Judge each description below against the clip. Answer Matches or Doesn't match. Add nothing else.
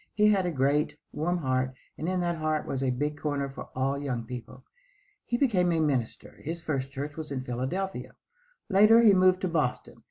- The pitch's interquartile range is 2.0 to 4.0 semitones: Doesn't match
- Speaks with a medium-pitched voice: Matches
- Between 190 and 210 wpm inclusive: Matches